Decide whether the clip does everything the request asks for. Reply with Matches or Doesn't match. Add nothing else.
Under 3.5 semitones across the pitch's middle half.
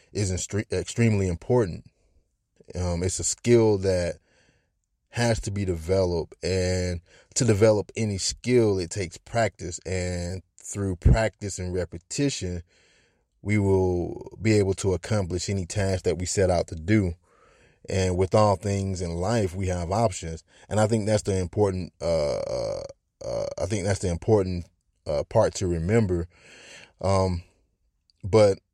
Matches